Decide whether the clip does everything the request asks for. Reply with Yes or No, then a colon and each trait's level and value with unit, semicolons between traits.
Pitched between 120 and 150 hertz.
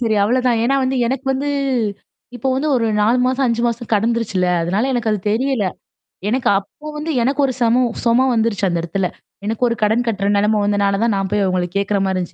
No: high, 230 Hz